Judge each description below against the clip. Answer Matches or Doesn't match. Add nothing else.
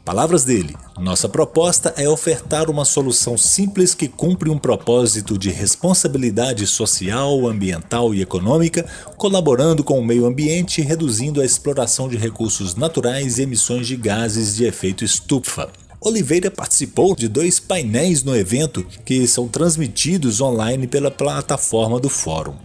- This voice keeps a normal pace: Matches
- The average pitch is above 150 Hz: Doesn't match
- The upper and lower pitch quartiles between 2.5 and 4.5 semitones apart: Doesn't match